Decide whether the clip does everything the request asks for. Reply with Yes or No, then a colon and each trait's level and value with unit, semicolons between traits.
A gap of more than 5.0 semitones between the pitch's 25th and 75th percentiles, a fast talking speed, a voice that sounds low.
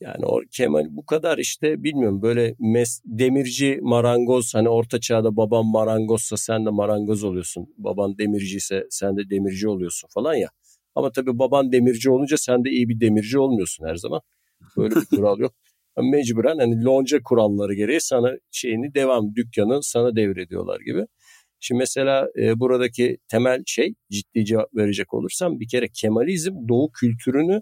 No: average, 3.5 semitones; fast, 160 wpm; low, 115 Hz